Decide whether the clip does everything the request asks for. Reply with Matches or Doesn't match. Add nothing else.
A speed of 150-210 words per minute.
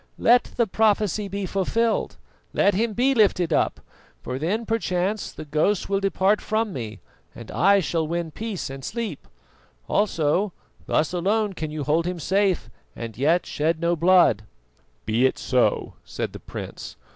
Matches